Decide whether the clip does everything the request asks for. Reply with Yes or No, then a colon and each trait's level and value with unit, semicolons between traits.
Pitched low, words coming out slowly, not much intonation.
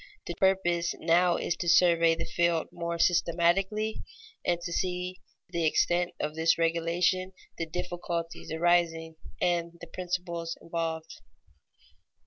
No: medium, 170 Hz; slow, 120 wpm; narrow, 1.2 semitones